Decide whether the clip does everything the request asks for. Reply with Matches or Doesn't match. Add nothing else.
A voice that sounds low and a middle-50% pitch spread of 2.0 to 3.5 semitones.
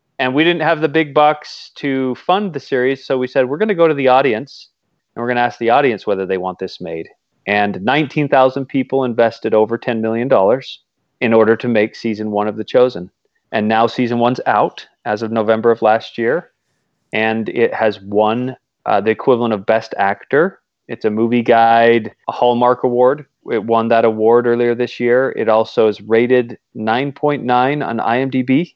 Matches